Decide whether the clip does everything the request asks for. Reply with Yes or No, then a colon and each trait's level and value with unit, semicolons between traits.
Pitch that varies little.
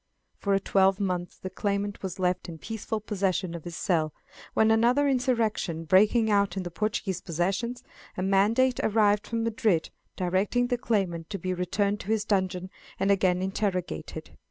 No: average, 3.1 semitones